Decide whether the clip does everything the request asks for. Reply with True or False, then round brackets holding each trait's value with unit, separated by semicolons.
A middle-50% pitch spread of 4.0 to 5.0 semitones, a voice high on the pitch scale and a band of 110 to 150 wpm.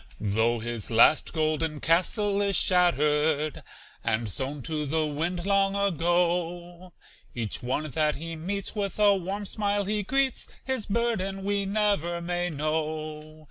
False (4.6 semitones; 170 Hz; 140 wpm)